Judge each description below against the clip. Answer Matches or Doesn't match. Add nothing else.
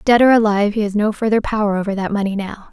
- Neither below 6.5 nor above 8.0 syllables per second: Matches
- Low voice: Doesn't match